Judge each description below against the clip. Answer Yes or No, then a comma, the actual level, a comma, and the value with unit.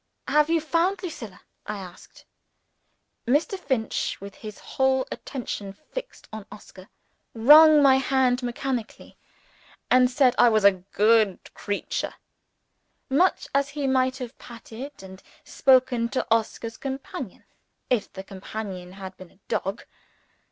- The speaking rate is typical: No, slow, 130 wpm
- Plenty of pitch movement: No, average, 4.9 semitones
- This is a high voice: Yes, high, 245 Hz